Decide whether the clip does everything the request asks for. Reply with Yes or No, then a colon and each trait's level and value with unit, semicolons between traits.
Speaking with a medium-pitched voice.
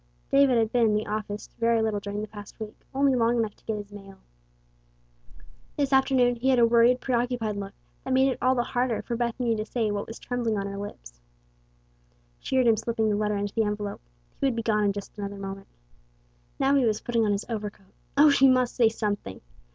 No: high, 225 Hz